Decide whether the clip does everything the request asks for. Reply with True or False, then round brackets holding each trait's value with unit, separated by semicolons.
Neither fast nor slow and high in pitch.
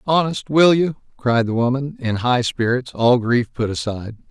False (180 wpm; 125 Hz)